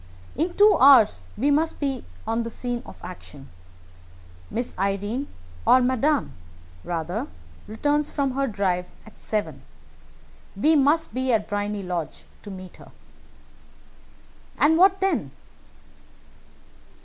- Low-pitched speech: No, high, 240 Hz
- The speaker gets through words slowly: Yes, slow, 120 wpm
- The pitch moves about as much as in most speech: No, wide, 6.5 semitones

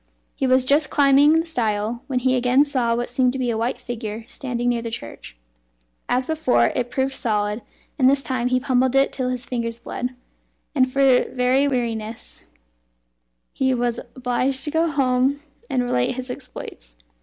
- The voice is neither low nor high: No, very high, 255 Hz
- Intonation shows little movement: Yes, narrow, 2.0 semitones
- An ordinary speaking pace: Yes, average, 175 wpm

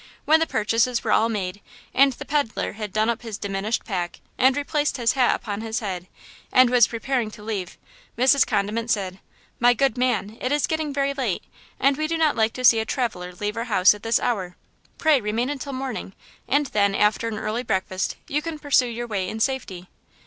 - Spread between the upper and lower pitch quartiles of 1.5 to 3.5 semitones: No, average, 4.3 semitones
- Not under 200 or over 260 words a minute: Yes, fast, 205 wpm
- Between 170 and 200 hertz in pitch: No, high, 230 Hz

